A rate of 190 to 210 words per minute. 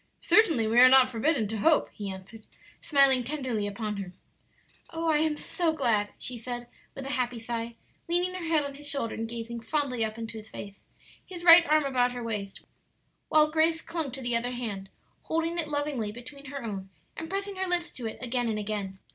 Yes: fast, 205 wpm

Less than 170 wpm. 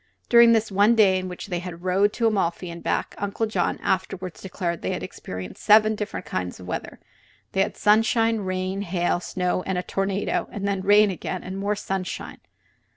No: average, 185 wpm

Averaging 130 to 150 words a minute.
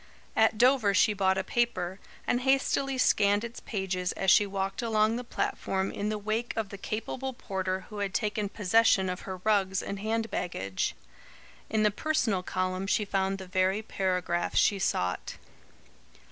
No: average, 165 wpm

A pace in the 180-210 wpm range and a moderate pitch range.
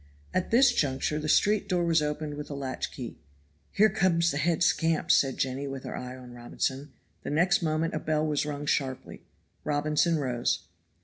Yes: average, 185 wpm; average, 3.3 semitones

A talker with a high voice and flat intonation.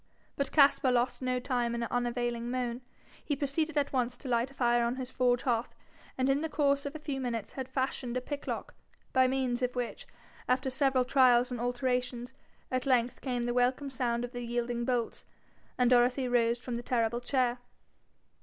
Yes: very high, 250 Hz; narrow, 1.5 semitones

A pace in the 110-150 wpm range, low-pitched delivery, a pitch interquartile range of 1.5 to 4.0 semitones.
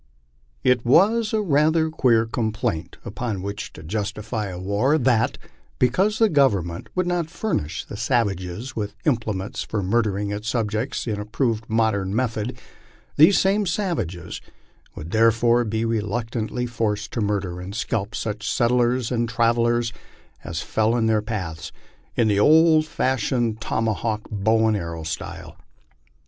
Yes: average, 145 wpm; low, 115 Hz; average, 3.3 semitones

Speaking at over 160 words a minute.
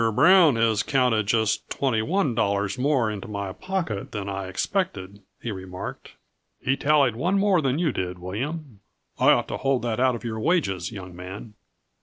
Yes: average, 175 wpm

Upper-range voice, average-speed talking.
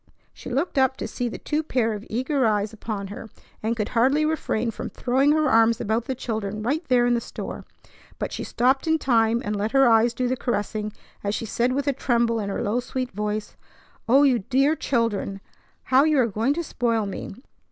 No: high, 235 Hz; fast, 215 wpm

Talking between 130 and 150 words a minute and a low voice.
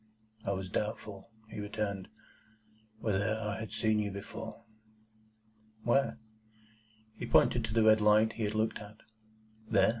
Yes: average, 140 wpm; low, 110 Hz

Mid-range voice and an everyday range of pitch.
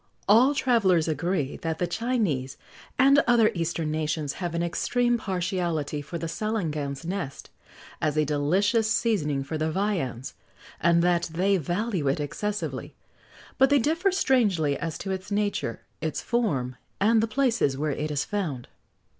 No: medium, 175 Hz; wide, 6.2 semitones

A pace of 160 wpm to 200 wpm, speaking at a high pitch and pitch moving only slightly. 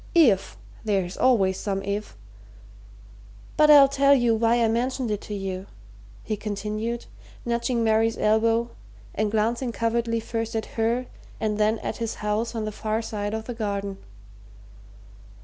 No: average, 150 wpm; high, 225 Hz; narrow, 1.9 semitones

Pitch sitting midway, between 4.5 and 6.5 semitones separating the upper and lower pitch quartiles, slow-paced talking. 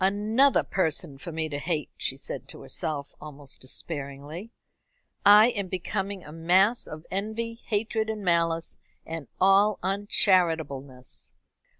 Yes: medium, 180 Hz; average, 5.1 semitones; slow, 125 wpm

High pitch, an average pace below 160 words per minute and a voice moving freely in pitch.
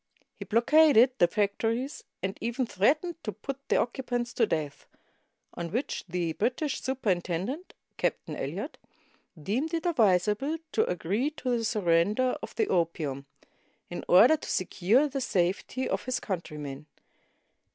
Yes: high, 225 Hz; average, 150 wpm; wide, 6.8 semitones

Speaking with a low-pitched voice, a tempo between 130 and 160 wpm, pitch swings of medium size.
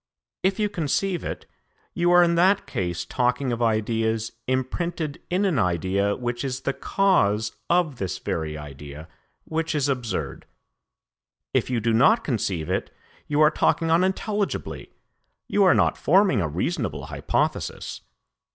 No: low, 130 Hz; average, 140 wpm; wide, 8.6 semitones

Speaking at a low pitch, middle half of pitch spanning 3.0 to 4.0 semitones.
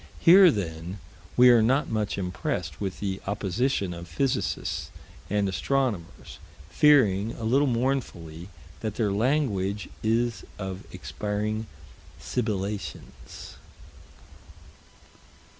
No: low, 105 Hz; average, 4.4 semitones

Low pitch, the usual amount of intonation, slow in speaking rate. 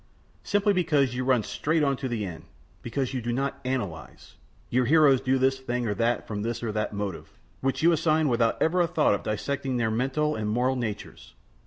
No: low, 130 Hz; average, 3.6 semitones; fast, 205 wpm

